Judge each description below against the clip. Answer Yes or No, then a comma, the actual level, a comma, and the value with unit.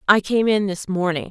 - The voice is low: No, high, 195 Hz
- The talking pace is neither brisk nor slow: No, fast, 230 wpm